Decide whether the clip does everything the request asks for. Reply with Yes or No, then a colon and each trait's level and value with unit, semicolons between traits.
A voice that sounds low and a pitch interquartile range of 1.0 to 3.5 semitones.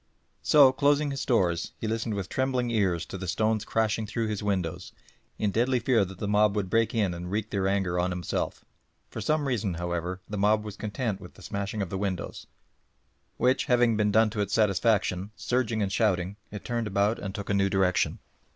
Yes: low, 105 Hz; average, 2.9 semitones